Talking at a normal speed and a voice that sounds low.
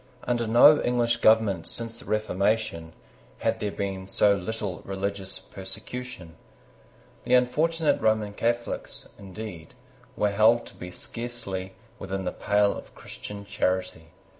No: slow, 125 wpm; low, 105 Hz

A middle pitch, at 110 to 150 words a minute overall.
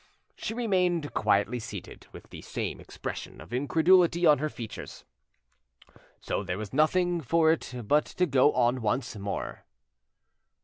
Yes: medium, 145 Hz; average, 140 wpm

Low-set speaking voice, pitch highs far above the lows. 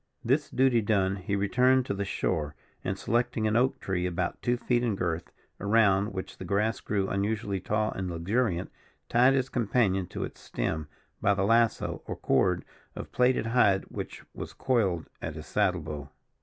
No: low, 100 Hz; average, 4.2 semitones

